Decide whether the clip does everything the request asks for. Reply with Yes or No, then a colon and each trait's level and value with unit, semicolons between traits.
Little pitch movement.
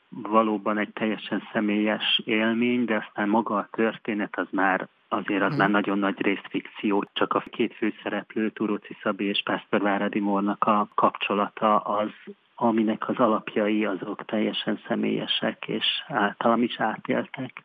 Yes: narrow, 1.5 semitones